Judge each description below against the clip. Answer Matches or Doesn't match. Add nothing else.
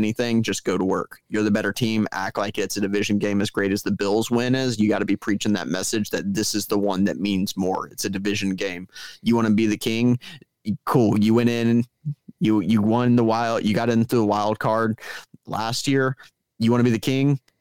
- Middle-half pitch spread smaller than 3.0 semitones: Matches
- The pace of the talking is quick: Matches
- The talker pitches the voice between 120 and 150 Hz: Doesn't match